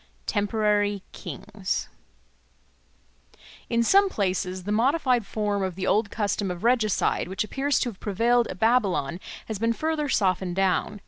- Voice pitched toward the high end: Yes, high, 210 Hz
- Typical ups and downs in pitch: Yes, average, 3.7 semitones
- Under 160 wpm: Yes, average, 140 wpm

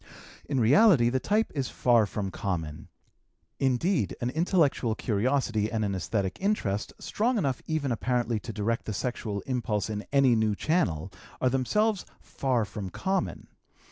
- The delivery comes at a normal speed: Yes, average, 145 wpm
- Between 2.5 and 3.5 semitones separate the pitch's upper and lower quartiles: No, average, 5.2 semitones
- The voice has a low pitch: Yes, low, 120 Hz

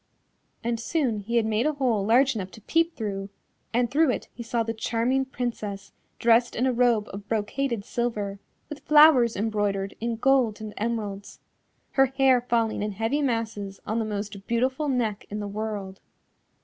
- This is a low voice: No, high, 230 Hz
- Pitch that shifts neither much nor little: Yes, average, 3.4 semitones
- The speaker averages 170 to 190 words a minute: Yes, average, 175 wpm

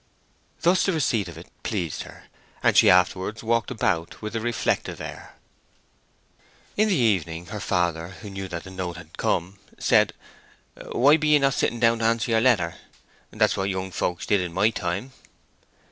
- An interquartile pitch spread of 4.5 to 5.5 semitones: Yes, average, 4.8 semitones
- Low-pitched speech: Yes, low, 100 Hz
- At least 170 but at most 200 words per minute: Yes, average, 175 wpm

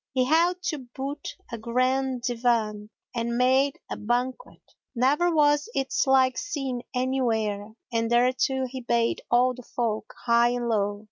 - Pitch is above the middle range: Yes, very high, 250 Hz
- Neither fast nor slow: Yes, average, 145 wpm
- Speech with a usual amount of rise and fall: No, narrow, 2.3 semitones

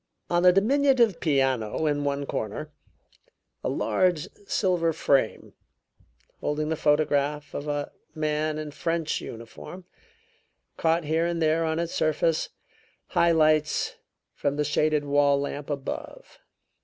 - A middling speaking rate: No, slow, 125 wpm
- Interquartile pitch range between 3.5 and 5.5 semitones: No, narrow, 2.4 semitones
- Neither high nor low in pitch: Yes, medium, 155 Hz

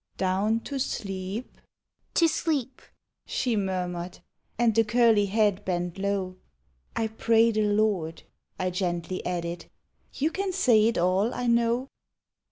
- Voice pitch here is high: Yes, high, 210 Hz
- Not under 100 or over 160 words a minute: Yes, average, 155 wpm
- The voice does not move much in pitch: No, average, 4.1 semitones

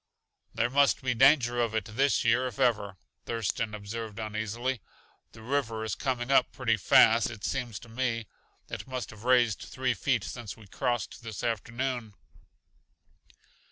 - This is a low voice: Yes, low, 115 Hz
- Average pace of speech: Yes, average, 155 wpm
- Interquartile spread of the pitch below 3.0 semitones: Yes, narrow, 2.5 semitones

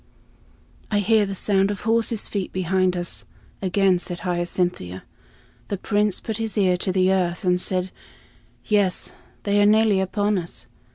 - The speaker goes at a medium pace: Yes, average, 155 wpm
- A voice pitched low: No, high, 190 Hz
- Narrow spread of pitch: Yes, narrow, 2.3 semitones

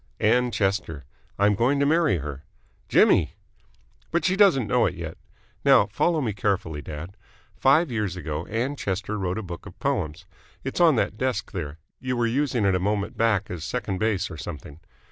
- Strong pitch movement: Yes, wide, 6.2 semitones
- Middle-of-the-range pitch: No, low, 105 Hz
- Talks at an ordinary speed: Yes, average, 185 wpm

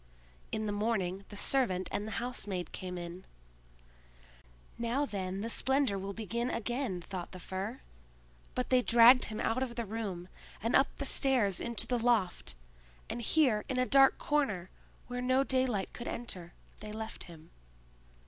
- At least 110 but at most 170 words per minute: Yes, average, 160 wpm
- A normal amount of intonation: Yes, average, 4.8 semitones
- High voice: Yes, high, 225 Hz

